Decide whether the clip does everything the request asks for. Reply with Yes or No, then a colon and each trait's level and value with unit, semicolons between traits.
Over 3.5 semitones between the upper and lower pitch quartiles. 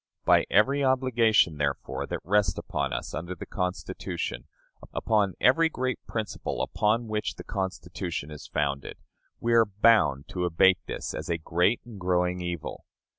Yes: average, 4.7 semitones